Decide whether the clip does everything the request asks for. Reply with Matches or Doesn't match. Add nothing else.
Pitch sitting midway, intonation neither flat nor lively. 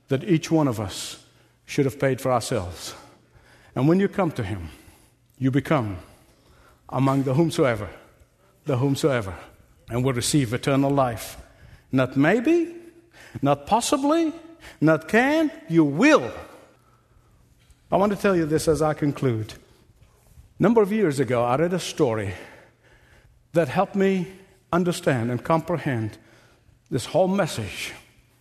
Doesn't match